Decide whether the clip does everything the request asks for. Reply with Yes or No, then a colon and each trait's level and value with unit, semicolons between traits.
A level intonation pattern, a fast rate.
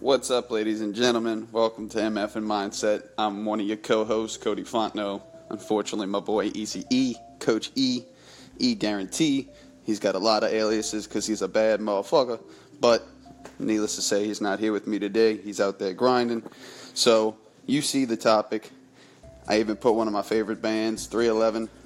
No: narrow, 1.5 semitones; average, 180 wpm